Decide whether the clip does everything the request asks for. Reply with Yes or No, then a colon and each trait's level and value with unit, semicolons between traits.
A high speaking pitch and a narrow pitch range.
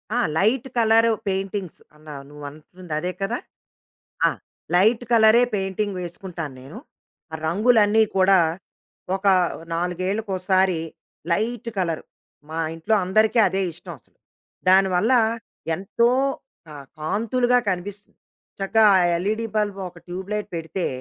No: high, 195 Hz; average, 3.6 semitones